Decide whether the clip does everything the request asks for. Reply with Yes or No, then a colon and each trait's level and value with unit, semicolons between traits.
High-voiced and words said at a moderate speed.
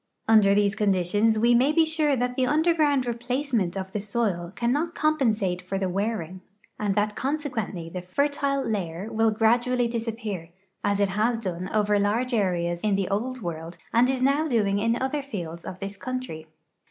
Yes: high, 220 Hz; average, 175 wpm